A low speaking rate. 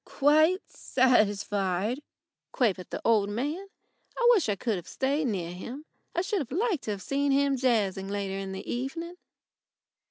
No: average, 155 wpm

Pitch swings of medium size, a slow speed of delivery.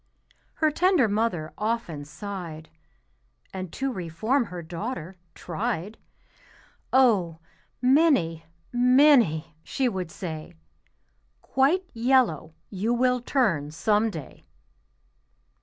No: wide, 7.2 semitones; slow, 90 wpm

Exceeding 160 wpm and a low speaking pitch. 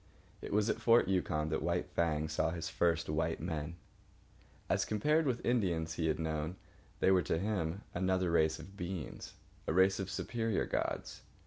Yes: average, 180 wpm; very low, 85 Hz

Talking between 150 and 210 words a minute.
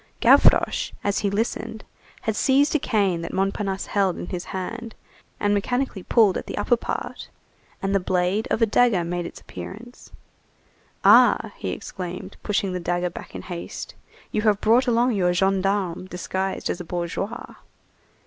Yes: average, 160 wpm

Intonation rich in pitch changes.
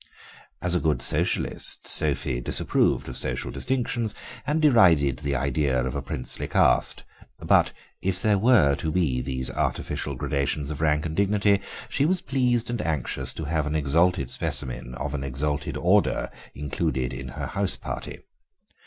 Yes: wide, 6.7 semitones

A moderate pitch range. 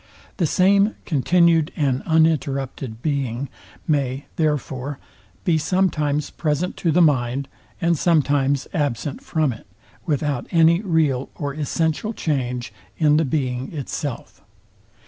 Yes: average, 3.2 semitones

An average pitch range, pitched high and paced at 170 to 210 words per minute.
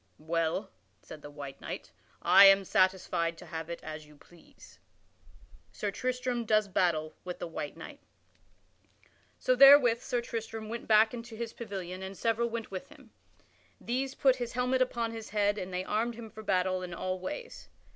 Yes: average, 4.6 semitones; high, 210 Hz; average, 175 wpm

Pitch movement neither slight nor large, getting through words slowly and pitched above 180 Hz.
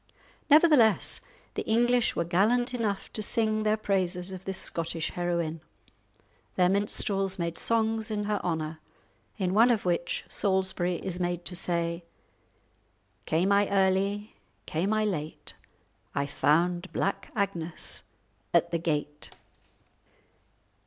Yes: average, 3.7 semitones; slow, 125 wpm; high, 190 Hz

